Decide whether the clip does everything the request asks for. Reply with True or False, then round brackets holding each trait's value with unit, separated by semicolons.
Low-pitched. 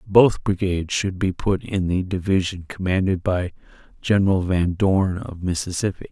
True (95 Hz)